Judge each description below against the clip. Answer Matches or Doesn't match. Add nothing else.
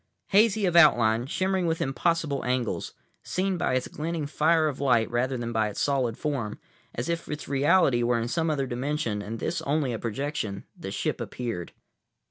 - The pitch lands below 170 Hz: Matches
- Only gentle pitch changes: Doesn't match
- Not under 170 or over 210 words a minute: Matches